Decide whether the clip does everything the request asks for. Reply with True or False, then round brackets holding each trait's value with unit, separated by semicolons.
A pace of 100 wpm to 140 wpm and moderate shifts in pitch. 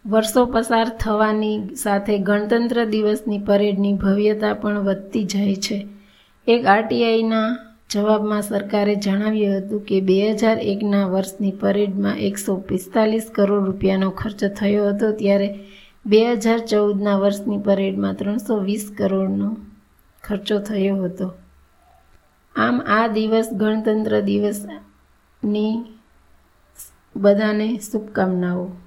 False (105 wpm; 1.7 semitones)